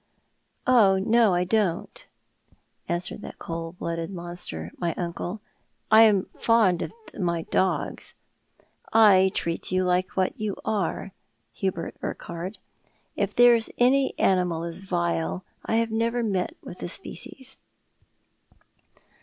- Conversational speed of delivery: No, slow, 130 wpm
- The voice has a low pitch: No, medium, 185 Hz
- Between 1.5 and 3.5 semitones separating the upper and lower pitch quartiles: No, average, 4.4 semitones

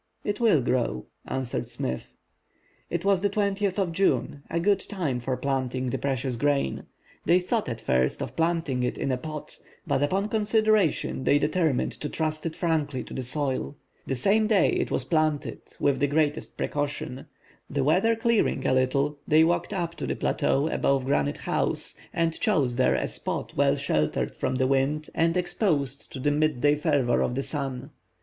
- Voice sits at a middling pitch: Yes, medium, 145 Hz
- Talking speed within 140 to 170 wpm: No, average, 180 wpm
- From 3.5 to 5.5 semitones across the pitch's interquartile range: Yes, average, 4.7 semitones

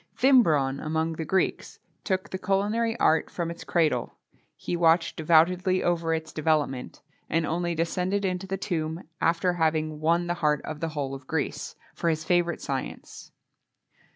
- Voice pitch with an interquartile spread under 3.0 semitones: Yes, narrow, 2.5 semitones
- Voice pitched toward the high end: No, medium, 165 Hz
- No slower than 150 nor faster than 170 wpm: Yes, average, 160 wpm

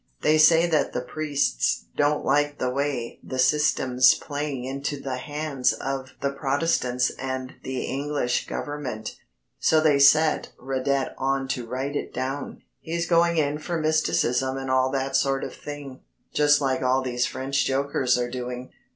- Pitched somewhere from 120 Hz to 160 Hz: Yes, low, 135 Hz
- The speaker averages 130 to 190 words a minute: Yes, average, 160 wpm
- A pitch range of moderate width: No, narrow, 2.2 semitones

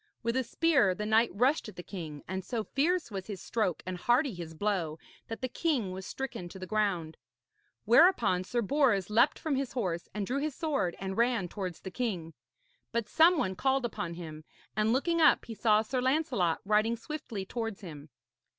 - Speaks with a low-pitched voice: No, high, 215 Hz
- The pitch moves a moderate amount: No, wide, 5.8 semitones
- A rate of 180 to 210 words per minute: Yes, average, 195 wpm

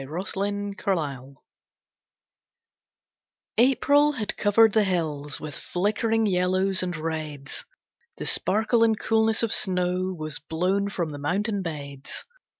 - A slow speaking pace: Yes, slow, 120 wpm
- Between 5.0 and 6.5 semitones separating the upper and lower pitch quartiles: Yes, average, 5.3 semitones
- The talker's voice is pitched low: No, medium, 185 Hz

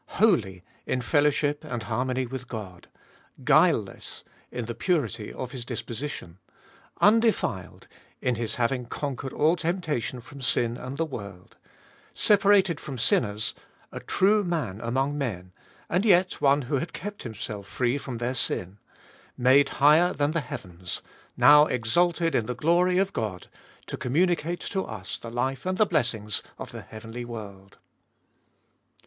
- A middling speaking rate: Yes, average, 145 wpm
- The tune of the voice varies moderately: No, wide, 6.4 semitones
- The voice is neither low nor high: No, low, 130 Hz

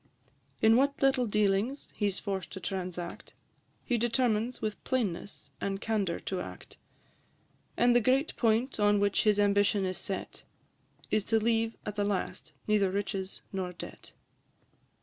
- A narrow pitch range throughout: No, average, 3.0 semitones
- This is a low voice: No, high, 210 Hz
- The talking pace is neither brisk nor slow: Yes, average, 150 wpm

